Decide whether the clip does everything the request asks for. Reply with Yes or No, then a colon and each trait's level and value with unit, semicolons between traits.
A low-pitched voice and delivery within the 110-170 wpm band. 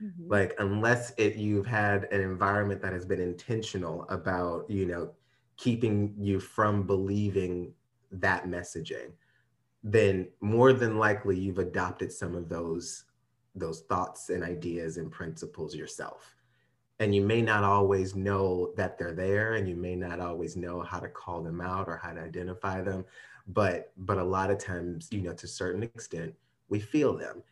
Yes: very low, 95 Hz; average, 165 wpm